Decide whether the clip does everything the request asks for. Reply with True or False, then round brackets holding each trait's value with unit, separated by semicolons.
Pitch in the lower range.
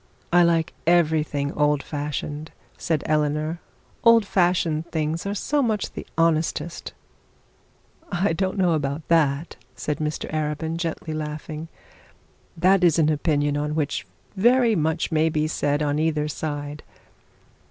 False (155 Hz)